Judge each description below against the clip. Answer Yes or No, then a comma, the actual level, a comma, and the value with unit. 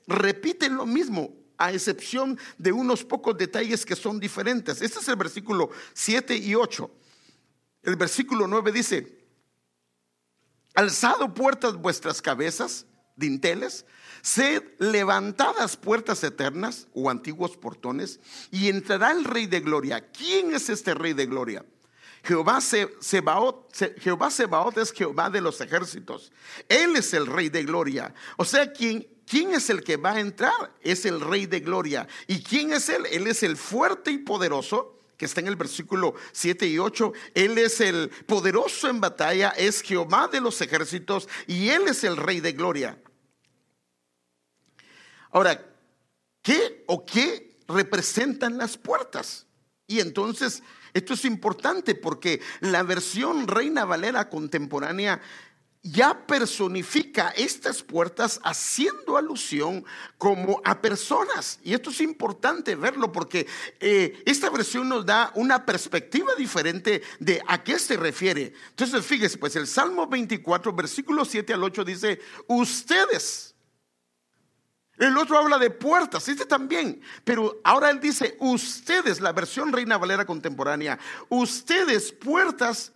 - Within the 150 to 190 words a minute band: No, slow, 135 wpm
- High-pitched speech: Yes, high, 225 Hz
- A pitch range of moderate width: No, wide, 6.2 semitones